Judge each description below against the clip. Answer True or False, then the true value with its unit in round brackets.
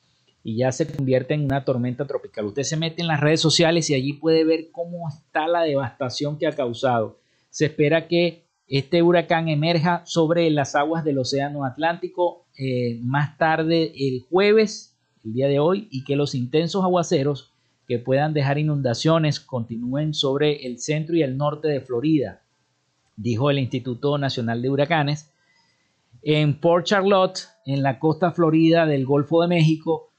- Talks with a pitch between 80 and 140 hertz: False (150 Hz)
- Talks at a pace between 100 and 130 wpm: False (165 wpm)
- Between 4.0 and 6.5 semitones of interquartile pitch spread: False (3.4 semitones)